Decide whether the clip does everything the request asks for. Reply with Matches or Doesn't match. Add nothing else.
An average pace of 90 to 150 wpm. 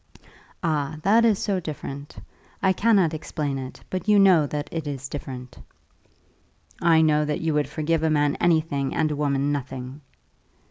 Doesn't match